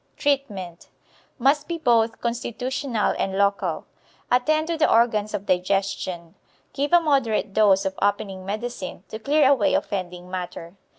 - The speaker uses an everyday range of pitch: No, wide, 5.8 semitones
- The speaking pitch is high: Yes, high, 215 Hz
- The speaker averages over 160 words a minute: No, slow, 135 wpm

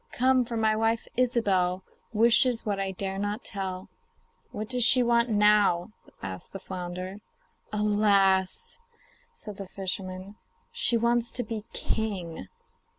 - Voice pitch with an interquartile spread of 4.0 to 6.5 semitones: No, average, 3.5 semitones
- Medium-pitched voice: No, high, 210 Hz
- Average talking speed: No, slow, 130 wpm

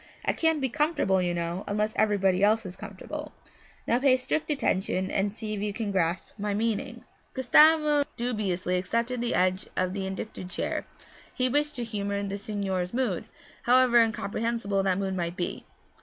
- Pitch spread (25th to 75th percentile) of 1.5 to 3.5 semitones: No, average, 4.2 semitones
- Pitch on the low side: No, high, 210 Hz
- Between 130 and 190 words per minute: Yes, average, 170 wpm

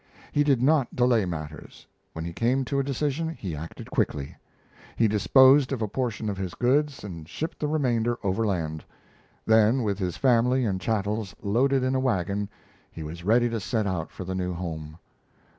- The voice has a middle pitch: No, low, 110 Hz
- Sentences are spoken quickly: No, average, 180 wpm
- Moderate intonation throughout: No, wide, 6.2 semitones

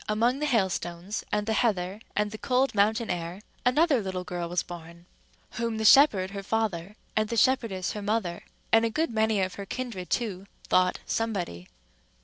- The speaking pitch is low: No, high, 210 Hz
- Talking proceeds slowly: No, average, 175 wpm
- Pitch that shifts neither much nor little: Yes, average, 3.9 semitones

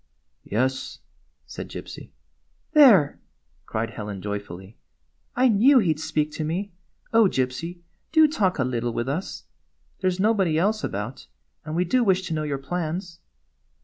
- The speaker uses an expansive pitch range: Yes, wide, 7.5 semitones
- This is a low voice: No, medium, 160 Hz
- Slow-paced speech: No, average, 165 wpm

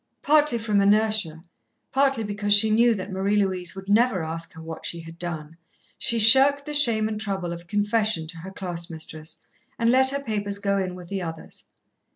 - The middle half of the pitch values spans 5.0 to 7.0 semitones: No, average, 4.4 semitones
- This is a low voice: No, high, 200 Hz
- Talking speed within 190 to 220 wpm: Yes, average, 195 wpm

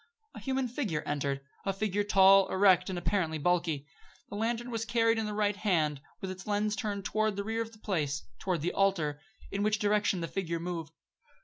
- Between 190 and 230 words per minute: Yes, average, 200 wpm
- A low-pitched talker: No, high, 195 Hz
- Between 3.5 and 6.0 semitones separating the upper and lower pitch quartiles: Yes, average, 3.8 semitones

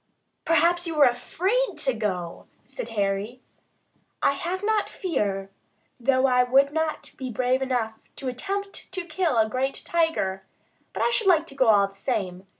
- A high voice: Yes, very high, 265 Hz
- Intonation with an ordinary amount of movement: No, wide, 7.4 semitones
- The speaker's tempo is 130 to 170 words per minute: Yes, average, 165 wpm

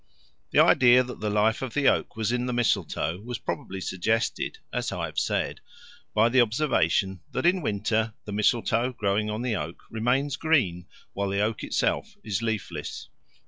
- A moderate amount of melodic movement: Yes, average, 3.4 semitones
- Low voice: Yes, low, 110 Hz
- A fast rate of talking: No, average, 175 wpm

